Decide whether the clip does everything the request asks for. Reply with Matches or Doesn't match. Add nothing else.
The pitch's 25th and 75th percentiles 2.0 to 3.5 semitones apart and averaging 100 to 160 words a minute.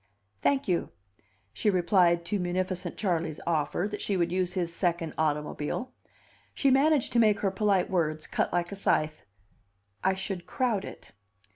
Matches